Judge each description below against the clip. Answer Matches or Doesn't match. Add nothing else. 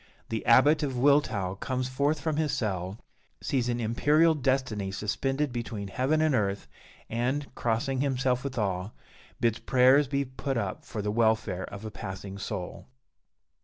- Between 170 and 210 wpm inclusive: Doesn't match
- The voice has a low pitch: Matches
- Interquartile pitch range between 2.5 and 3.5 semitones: Doesn't match